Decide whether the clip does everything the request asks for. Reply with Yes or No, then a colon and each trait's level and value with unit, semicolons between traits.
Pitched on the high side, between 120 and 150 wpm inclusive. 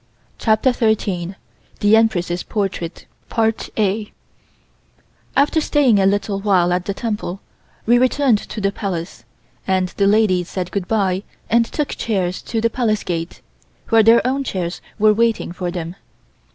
Yes: high, 205 Hz; average, 140 wpm